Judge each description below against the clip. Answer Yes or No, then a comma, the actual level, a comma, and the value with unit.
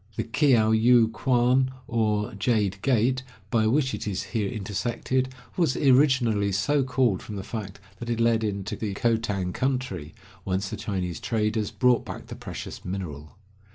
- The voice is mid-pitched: No, low, 110 Hz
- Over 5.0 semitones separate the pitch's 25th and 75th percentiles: No, average, 4.1 semitones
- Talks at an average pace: Yes, average, 155 wpm